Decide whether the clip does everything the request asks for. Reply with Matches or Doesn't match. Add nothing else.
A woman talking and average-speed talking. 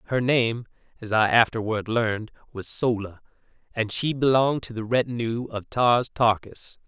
Doesn't match